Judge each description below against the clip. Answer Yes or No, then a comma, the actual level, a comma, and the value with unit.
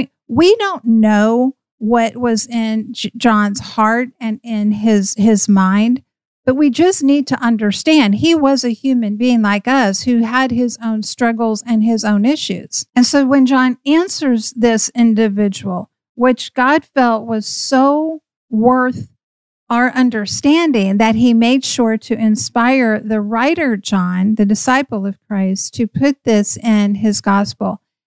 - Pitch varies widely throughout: No, average, 3.1 semitones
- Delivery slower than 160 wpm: Yes, average, 150 wpm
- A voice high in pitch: Yes, high, 230 Hz